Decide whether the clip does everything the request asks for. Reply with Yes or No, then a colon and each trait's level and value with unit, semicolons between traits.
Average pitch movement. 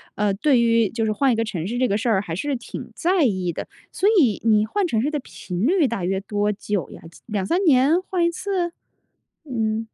No: wide, 6.2 semitones